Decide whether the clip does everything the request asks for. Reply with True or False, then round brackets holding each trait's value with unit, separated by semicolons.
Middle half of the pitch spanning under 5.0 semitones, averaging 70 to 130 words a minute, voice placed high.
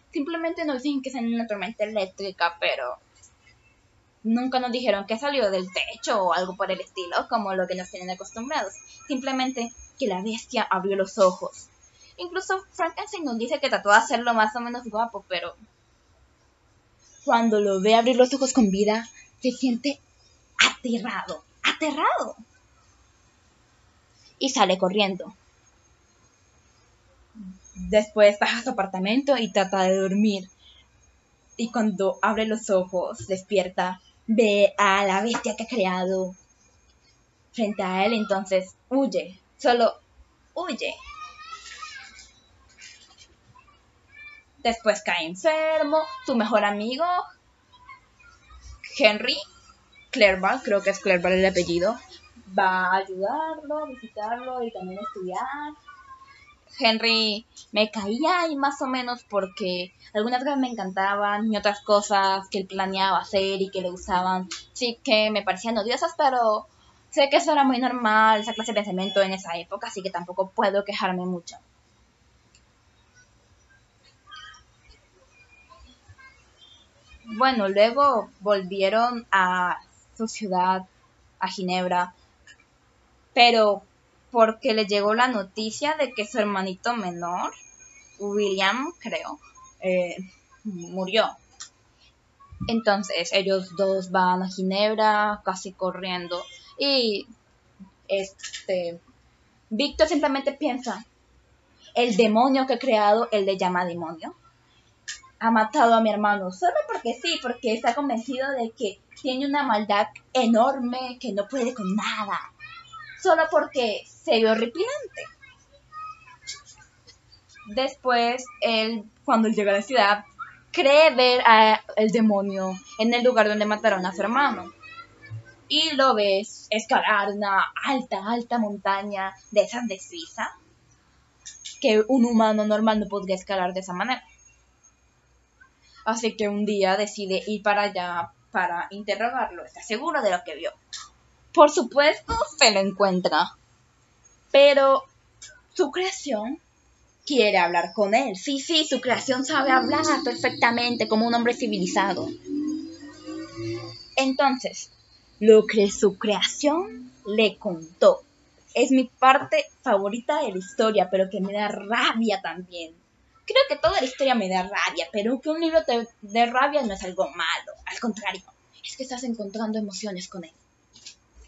False (5.4 semitones; 125 wpm; 220 Hz)